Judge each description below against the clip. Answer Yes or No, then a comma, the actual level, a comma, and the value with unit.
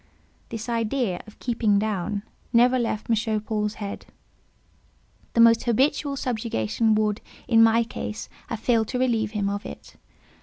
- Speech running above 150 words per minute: No, average, 145 wpm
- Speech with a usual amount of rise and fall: No, narrow, 1.9 semitones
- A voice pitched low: No, high, 225 Hz